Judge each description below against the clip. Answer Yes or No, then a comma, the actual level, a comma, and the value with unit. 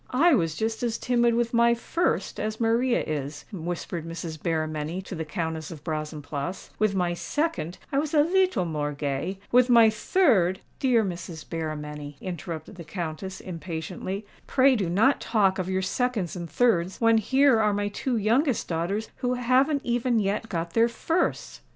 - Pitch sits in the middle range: No, high, 195 Hz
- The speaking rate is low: No, average, 165 wpm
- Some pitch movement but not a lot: No, wide, 6.3 semitones